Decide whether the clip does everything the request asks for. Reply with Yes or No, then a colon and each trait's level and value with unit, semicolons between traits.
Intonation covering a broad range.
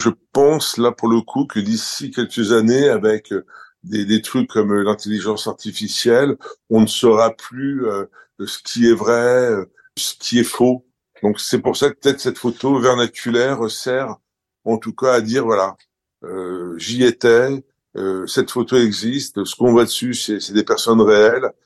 No: average, 2.9 semitones